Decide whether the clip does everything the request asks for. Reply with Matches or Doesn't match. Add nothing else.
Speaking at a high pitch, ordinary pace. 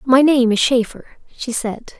Matches